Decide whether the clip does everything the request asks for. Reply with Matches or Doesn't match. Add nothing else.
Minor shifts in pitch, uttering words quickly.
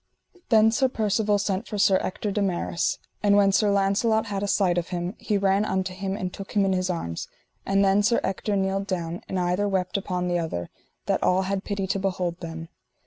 Matches